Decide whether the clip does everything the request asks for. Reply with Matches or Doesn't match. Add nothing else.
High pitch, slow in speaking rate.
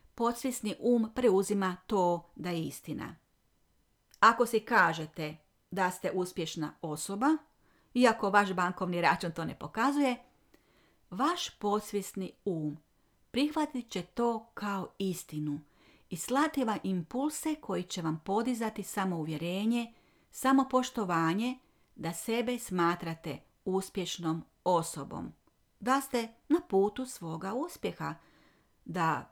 Matches